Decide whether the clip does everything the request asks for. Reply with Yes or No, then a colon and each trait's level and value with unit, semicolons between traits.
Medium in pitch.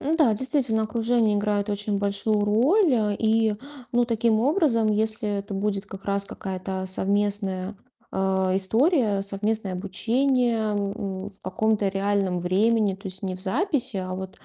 No: high, 205 Hz